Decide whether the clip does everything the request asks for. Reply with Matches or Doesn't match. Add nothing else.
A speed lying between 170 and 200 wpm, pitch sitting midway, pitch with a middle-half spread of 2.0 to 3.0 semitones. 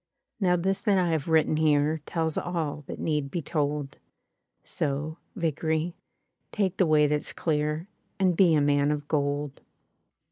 Doesn't match